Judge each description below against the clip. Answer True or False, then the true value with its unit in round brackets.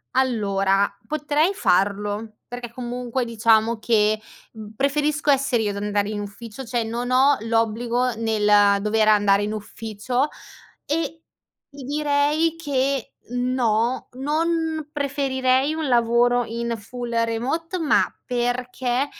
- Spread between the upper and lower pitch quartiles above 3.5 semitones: True (4.2 semitones)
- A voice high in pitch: True (245 Hz)